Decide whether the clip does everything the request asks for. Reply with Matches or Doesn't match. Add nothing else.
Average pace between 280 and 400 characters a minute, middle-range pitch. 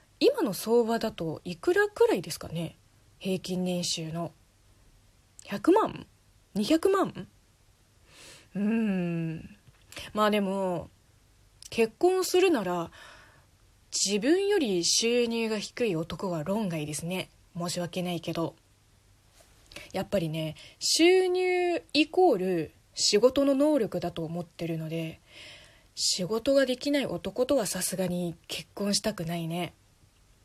Doesn't match